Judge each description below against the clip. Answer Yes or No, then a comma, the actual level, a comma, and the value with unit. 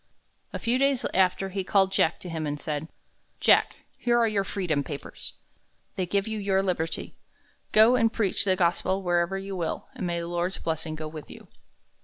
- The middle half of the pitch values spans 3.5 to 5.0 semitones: No, average, 3.0 semitones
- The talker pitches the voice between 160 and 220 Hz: Yes, medium, 185 Hz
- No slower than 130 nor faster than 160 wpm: No, average, 190 wpm